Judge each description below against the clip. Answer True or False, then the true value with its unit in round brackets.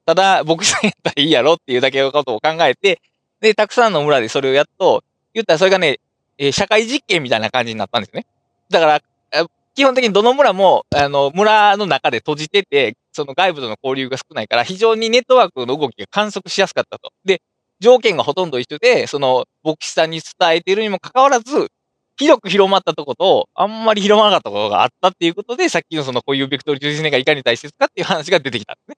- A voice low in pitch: False (185 Hz)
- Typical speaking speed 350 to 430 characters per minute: False (470 characters per minute)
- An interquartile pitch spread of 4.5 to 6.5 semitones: False (7.8 semitones)